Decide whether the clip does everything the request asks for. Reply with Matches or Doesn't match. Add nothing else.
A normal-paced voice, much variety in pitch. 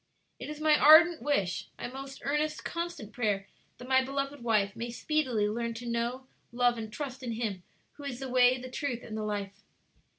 Doesn't match